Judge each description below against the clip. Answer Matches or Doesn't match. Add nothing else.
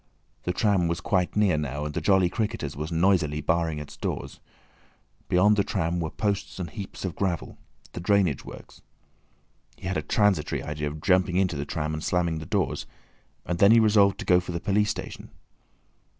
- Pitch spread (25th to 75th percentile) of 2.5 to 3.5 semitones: Doesn't match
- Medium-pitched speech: Doesn't match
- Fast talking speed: Doesn't match